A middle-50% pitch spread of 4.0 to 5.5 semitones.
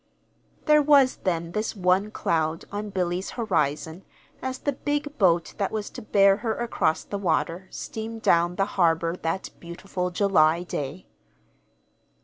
Yes: average, 4.4 semitones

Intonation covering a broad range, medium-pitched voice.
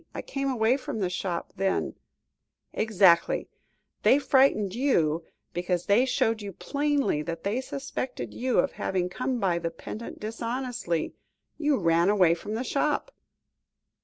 No: wide, 6.5 semitones; high, 215 Hz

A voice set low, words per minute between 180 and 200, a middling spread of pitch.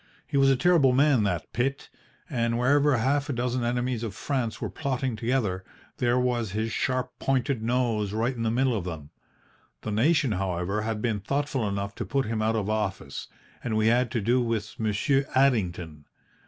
Yes: low, 120 Hz; average, 185 wpm; average, 3.5 semitones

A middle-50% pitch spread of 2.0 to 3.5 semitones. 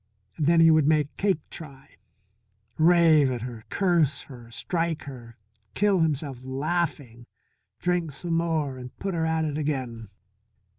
No: average, 4.1 semitones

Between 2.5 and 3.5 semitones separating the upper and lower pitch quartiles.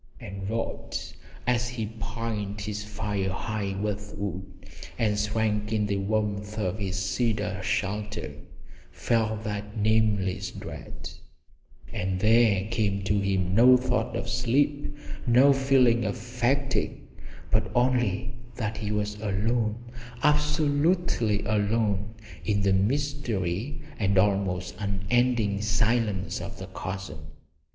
Yes: average, 3.0 semitones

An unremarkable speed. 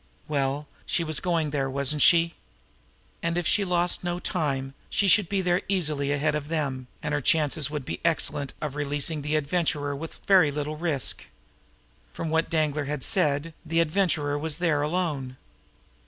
Yes: average, 170 wpm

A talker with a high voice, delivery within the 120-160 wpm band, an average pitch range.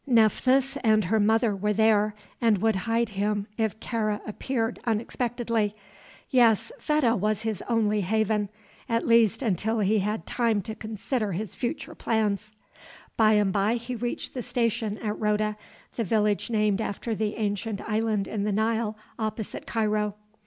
No: high, 220 Hz; average, 150 wpm; narrow, 1.6 semitones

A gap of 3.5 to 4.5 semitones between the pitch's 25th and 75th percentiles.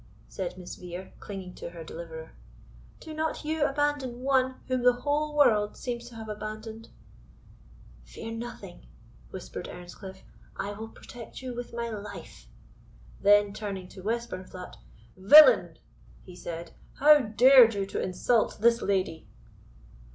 No: average, 5.0 semitones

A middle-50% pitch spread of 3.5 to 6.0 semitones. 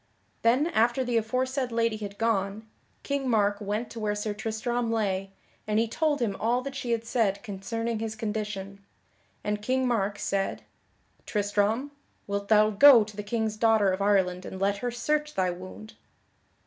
No: average, 2.8 semitones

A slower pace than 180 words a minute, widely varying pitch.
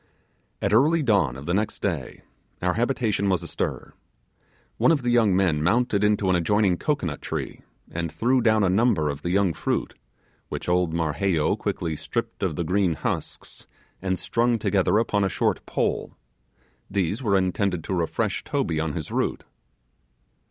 No: average, 165 wpm; average, 4.5 semitones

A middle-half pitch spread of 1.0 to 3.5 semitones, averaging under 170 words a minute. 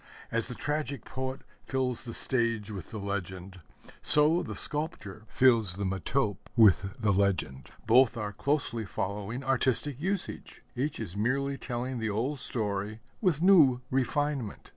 No: average, 5.1 semitones; average, 140 wpm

